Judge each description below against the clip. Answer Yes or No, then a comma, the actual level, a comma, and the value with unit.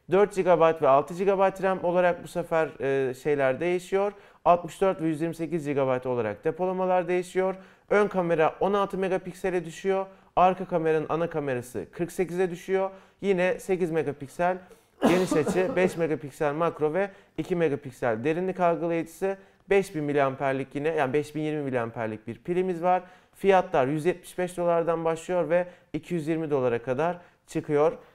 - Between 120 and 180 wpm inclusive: Yes, average, 130 wpm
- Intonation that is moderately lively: Yes, average, 3.3 semitones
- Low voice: No, medium, 175 Hz